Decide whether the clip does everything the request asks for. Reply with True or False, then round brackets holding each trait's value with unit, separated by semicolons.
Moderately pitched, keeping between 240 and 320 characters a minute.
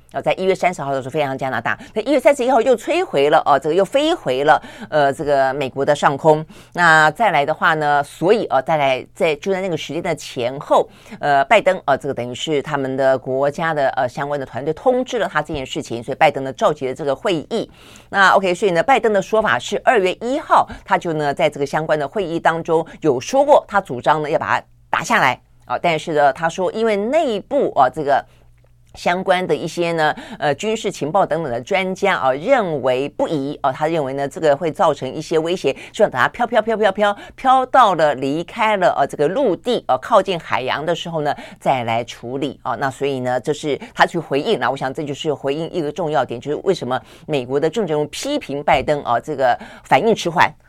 False (155 Hz; 330 characters per minute)